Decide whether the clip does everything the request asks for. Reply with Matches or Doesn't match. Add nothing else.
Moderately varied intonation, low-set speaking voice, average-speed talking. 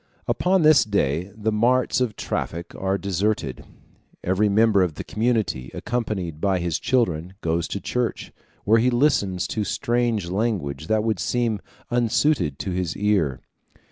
Matches